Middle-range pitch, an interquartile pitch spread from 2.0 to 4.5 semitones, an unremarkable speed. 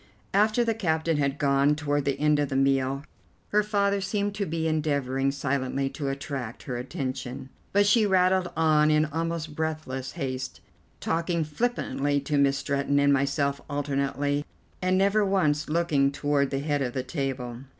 Yes: medium, 145 Hz; average, 3.3 semitones; average, 160 wpm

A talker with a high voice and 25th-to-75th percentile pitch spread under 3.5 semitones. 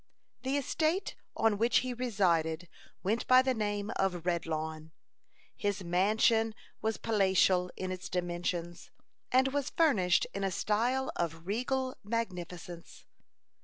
No: high, 200 Hz; average, 5.2 semitones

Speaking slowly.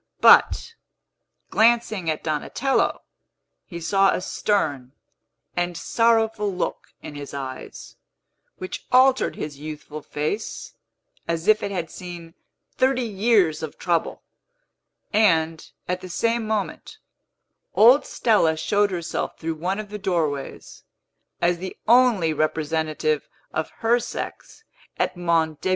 Yes: slow, 120 wpm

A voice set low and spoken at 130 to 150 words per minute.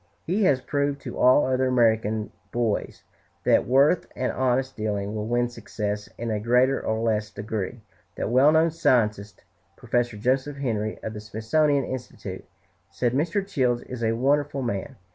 No: low, 120 Hz; average, 160 wpm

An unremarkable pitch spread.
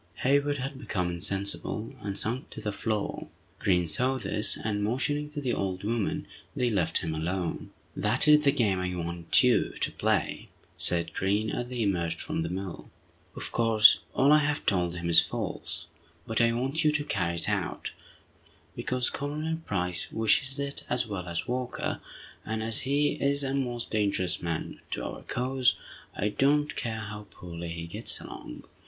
No: wide, 6.6 semitones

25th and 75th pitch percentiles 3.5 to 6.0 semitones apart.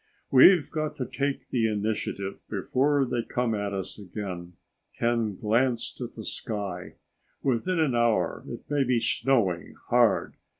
Yes: average, 4.6 semitones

